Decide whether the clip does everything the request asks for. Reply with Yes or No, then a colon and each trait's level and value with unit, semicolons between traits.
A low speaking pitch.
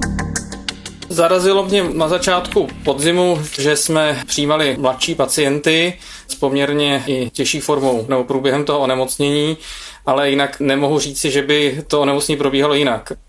No: medium, 145 Hz